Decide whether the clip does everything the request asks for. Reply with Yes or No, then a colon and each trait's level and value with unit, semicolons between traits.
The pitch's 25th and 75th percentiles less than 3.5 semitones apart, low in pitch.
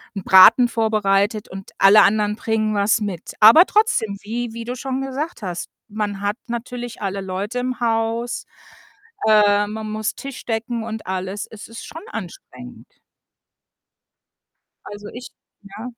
No: average, 2.7 semitones; high, 215 Hz